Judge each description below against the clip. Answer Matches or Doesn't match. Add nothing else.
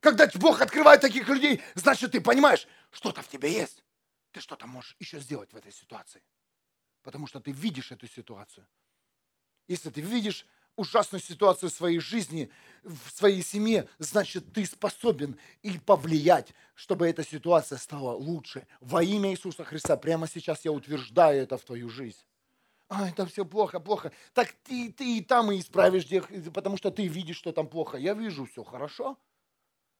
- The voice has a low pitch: Doesn't match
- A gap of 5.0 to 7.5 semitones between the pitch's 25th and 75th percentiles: Matches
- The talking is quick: Matches